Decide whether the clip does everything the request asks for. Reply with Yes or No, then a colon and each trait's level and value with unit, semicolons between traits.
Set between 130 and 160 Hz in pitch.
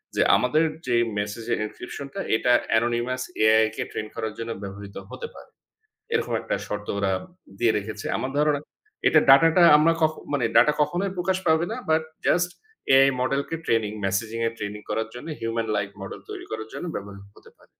No: low, 120 Hz